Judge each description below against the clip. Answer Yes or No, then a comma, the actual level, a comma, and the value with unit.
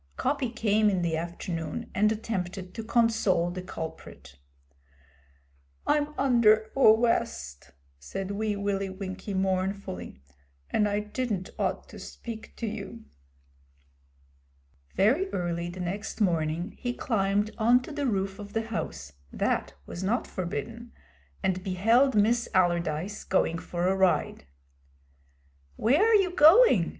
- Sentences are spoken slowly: Yes, slow, 125 wpm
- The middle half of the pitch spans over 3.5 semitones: Yes, average, 4.2 semitones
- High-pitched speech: Yes, high, 200 Hz